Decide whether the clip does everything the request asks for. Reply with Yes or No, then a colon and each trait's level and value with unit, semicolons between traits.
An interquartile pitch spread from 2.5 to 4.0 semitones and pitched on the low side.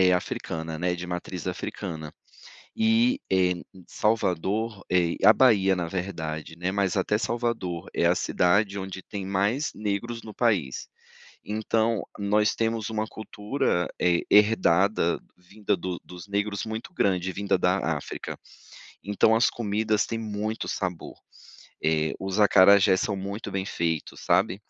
Yes: average, 3.3 semitones; low, 100 Hz